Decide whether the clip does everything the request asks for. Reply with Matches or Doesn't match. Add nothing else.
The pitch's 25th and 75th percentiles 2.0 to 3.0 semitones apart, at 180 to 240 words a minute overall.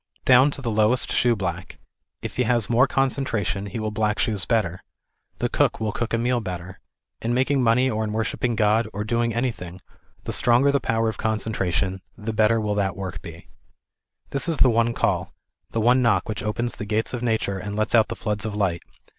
Matches